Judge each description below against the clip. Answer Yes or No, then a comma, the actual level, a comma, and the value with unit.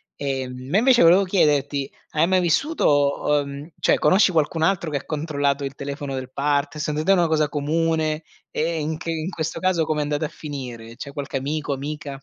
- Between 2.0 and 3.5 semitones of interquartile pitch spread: Yes, narrow, 2.6 semitones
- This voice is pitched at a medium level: Yes, medium, 150 Hz